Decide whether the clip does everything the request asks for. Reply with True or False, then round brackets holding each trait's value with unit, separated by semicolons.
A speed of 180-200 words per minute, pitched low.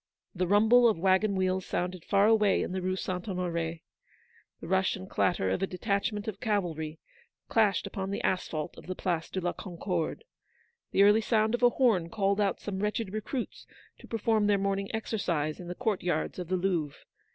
False (190 wpm; 190 Hz)